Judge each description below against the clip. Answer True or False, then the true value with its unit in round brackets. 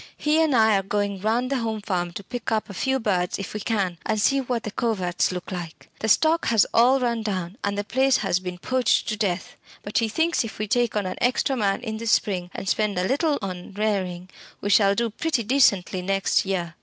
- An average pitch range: True (4.1 semitones)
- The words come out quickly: True (230 wpm)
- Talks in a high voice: True (210 Hz)